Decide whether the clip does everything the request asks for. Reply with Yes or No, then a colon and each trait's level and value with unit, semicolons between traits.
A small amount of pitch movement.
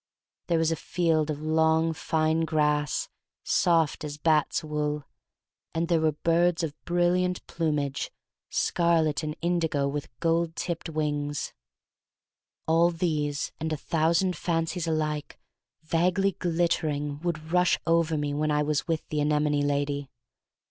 Yes: narrow, 2.1 semitones